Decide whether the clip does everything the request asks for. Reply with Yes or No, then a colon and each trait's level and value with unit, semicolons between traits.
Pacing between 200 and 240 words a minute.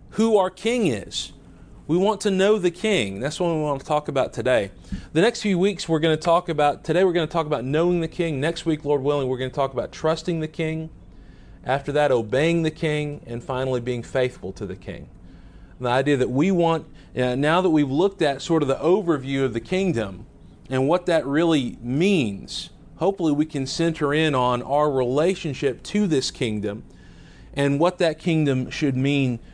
Yes: fast, 205 wpm